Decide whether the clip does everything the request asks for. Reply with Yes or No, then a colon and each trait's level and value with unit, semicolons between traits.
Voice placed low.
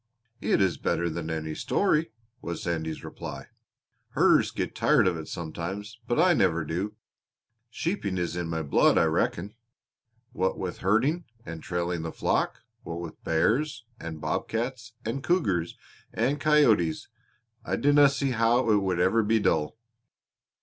Yes: very low, 95 Hz